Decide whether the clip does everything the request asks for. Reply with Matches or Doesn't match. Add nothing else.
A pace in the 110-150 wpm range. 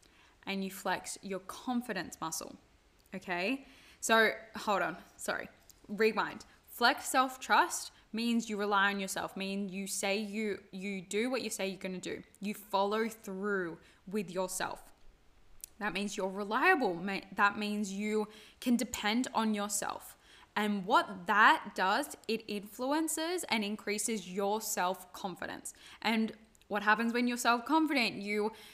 Matches